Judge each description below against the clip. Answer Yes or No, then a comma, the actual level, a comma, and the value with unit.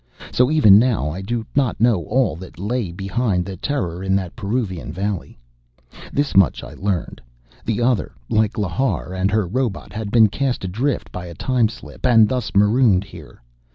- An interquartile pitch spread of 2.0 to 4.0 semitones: No, average, 4.6 semitones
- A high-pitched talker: No, low, 105 Hz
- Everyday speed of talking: Yes, average, 175 wpm